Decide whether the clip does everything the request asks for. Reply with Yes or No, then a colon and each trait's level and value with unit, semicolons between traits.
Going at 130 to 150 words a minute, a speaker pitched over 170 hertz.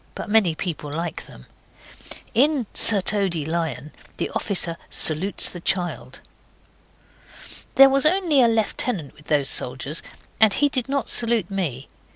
Yes: average, 140 wpm; high, 190 Hz